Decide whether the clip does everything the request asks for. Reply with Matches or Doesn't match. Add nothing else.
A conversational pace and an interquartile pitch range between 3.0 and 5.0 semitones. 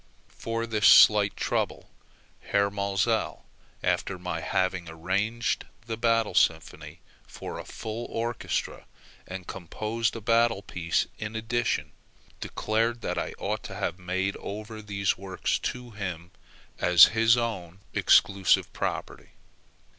Doesn't match